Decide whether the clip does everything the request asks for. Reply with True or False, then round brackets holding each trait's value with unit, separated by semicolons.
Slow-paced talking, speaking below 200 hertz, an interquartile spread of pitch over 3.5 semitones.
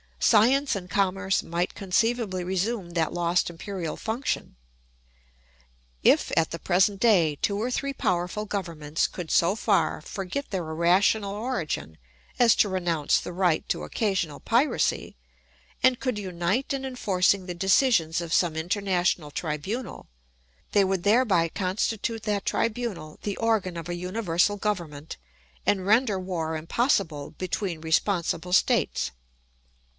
True (130 wpm; 190 Hz; 4.0 semitones)